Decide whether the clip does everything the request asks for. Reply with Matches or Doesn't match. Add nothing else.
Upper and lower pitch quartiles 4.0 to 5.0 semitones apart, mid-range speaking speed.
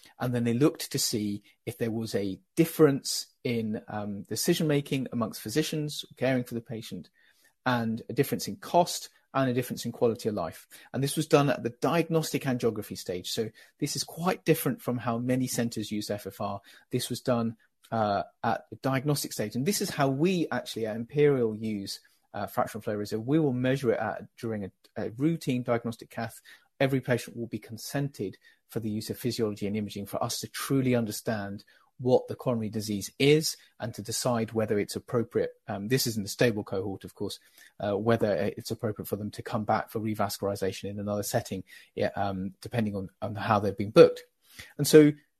Matches